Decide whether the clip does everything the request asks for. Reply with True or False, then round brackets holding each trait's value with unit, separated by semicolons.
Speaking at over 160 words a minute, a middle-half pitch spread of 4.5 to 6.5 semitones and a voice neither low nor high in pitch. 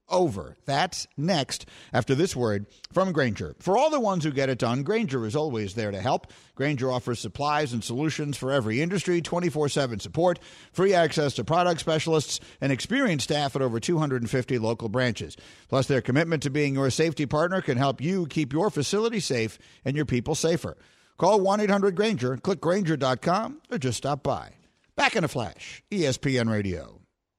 True (170 wpm; 5.3 semitones; 145 Hz)